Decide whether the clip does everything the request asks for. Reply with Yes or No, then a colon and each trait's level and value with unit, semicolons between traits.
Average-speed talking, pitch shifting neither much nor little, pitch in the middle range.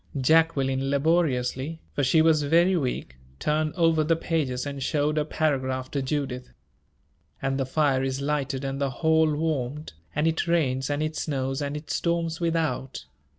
Yes: average, 160 wpm; average, 3.1 semitones; medium, 145 Hz